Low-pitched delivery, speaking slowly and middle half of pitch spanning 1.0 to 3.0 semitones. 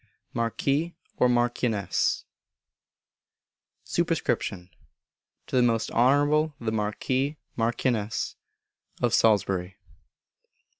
No: low, 120 Hz; slow, 70 wpm; average, 3.8 semitones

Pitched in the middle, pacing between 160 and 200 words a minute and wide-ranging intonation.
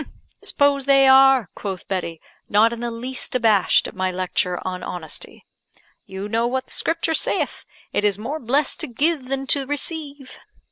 No: very high, 250 Hz; average, 170 wpm; wide, 5.7 semitones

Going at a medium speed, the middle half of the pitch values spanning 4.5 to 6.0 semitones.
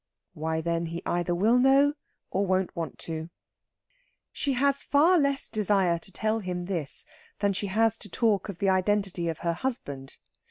Yes: average, 170 wpm; average, 4.9 semitones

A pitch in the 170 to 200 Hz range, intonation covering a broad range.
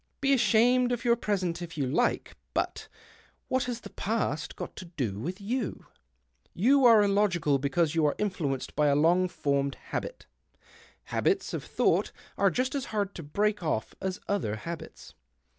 Yes: high, 190 Hz; wide, 7.4 semitones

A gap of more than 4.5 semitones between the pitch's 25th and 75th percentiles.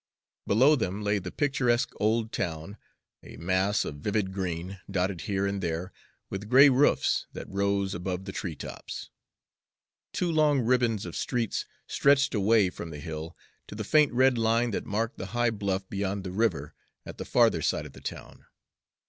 No: average, 4.1 semitones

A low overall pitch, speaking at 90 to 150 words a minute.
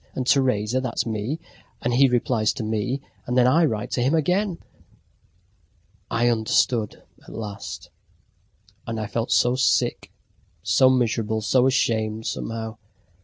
Yes: low, 120 Hz; slow, 135 wpm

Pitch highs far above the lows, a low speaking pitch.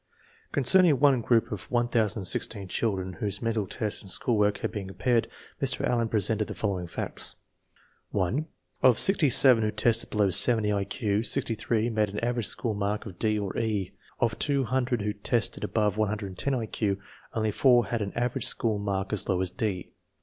No: average, 2.9 semitones; low, 110 Hz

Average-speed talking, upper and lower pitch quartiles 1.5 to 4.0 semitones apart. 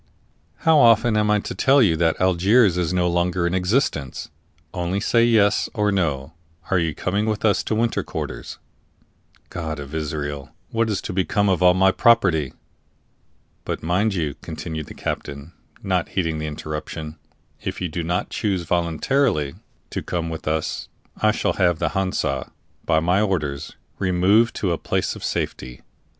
No: average, 165 wpm; average, 4.5 semitones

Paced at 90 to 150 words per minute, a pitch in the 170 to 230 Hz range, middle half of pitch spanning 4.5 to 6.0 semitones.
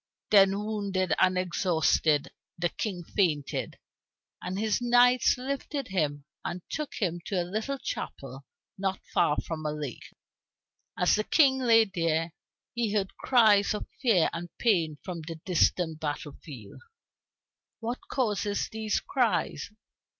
Yes: slow, 135 wpm; high, 190 Hz; average, 5.1 semitones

